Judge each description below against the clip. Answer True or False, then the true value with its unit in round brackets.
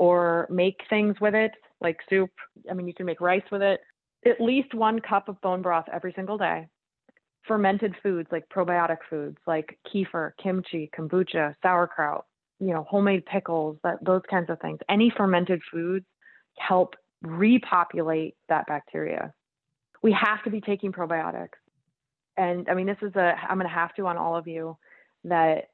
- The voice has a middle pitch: True (180 Hz)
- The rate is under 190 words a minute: True (170 wpm)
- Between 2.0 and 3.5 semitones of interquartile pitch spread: True (3.1 semitones)